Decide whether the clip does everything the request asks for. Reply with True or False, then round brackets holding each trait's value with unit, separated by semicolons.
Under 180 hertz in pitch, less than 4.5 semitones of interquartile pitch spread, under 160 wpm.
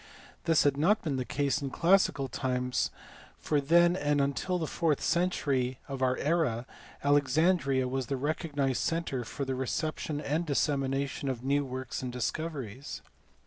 True (140 Hz; 3.2 semitones; 150 wpm)